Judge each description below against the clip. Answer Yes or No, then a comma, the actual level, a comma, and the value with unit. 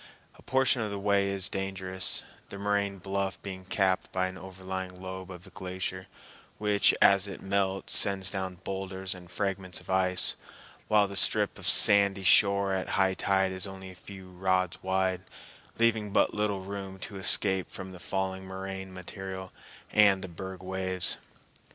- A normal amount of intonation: No, narrow, 0.9 semitones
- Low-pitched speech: Yes, very low, 95 Hz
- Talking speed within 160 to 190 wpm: Yes, average, 165 wpm